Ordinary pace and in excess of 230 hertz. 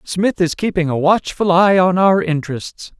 No: average, 180 wpm; medium, 180 Hz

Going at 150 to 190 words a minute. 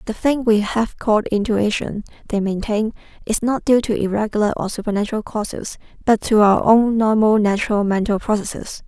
Yes: average, 160 wpm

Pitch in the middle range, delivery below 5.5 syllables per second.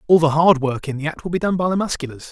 No: medium, 160 Hz; 6.6 syllables/s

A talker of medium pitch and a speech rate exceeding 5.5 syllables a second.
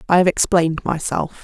Yes: medium, 170 Hz; 5.8 syllables/s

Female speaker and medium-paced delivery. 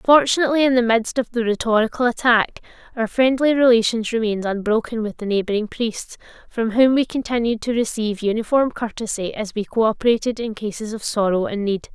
Yes: female; average, 170 wpm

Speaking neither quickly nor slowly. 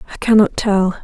Yes: average, 175 wpm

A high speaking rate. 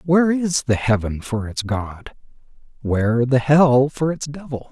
No: average, 165 wpm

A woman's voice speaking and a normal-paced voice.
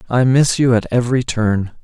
No: male; average, 195 wpm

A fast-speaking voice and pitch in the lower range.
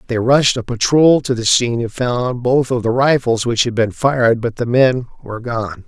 Yes: fast, 225 wpm; low, 120 Hz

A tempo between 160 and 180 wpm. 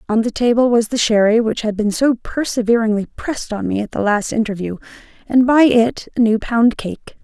No: fast, 205 wpm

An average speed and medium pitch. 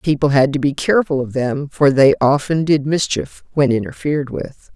Yes: average, 190 wpm; medium, 145 Hz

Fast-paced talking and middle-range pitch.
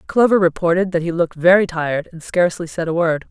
Yes: fast, 220 wpm; medium, 170 Hz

